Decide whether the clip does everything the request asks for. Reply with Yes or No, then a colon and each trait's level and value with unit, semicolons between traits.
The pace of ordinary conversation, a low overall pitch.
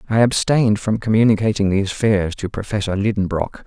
Yes: average, 145 wpm; low, 105 Hz